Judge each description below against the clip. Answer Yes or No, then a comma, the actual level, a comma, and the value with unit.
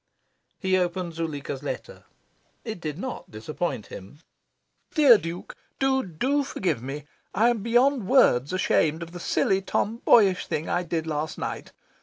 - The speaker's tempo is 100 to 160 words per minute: Yes, average, 145 wpm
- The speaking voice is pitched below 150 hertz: No, medium, 180 Hz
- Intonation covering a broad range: Yes, wide, 6.9 semitones